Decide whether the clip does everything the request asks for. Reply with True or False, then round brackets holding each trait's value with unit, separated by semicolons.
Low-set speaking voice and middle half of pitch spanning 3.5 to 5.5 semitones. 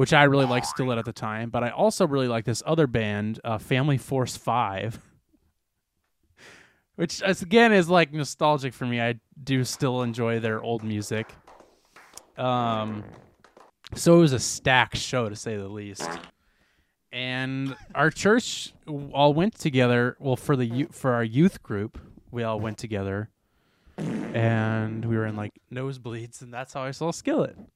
True (125 Hz; 4.1 semitones)